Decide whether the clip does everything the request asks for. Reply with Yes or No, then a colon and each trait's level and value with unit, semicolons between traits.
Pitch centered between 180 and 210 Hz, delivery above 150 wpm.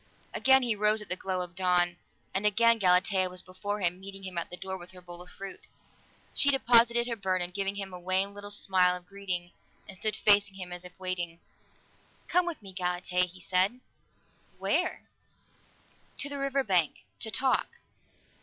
Yes: high, 190 Hz; average, 180 wpm